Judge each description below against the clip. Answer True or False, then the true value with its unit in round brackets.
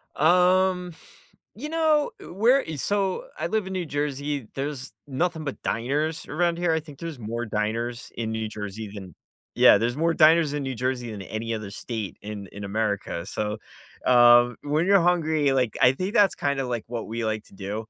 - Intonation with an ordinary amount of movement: False (7.1 semitones)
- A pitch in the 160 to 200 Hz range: False (135 Hz)